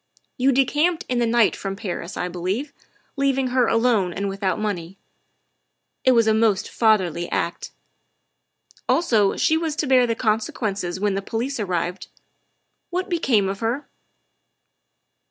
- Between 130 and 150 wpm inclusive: Yes, average, 145 wpm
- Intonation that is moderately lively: Yes, average, 4.9 semitones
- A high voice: Yes, high, 225 Hz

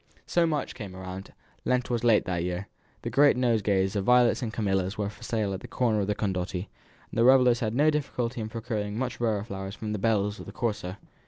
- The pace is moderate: No, fast, 225 wpm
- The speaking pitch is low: Yes, low, 110 Hz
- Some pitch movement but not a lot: Yes, average, 3.6 semitones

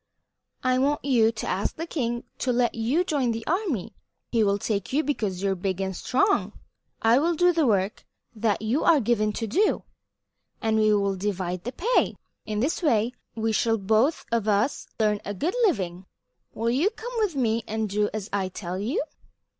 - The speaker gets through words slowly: No, average, 195 wpm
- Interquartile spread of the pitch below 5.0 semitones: No, average, 5.3 semitones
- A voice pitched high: Yes, high, 225 Hz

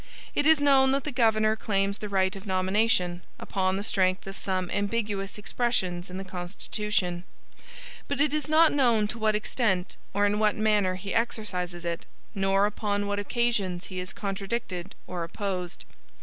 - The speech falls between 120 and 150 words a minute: No, average, 165 wpm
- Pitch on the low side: No, high, 205 Hz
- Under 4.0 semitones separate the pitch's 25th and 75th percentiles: Yes, average, 3.0 semitones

